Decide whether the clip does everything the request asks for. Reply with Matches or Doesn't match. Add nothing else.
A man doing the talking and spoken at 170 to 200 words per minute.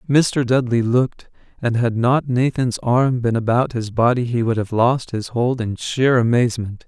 Matches